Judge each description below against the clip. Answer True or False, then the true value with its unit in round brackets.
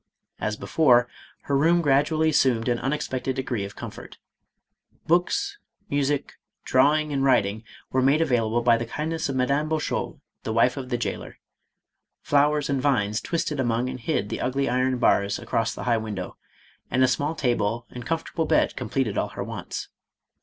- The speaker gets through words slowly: False (170 wpm)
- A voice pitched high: False (130 Hz)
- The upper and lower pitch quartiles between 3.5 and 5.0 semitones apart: True (4.0 semitones)